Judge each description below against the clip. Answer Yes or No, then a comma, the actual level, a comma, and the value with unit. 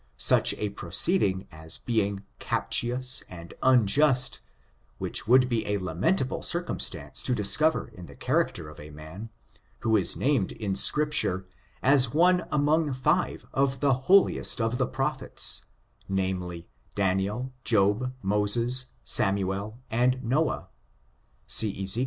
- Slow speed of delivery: Yes, slow, 130 wpm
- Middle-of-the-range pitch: No, low, 115 Hz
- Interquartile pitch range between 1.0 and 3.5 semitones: No, average, 5.3 semitones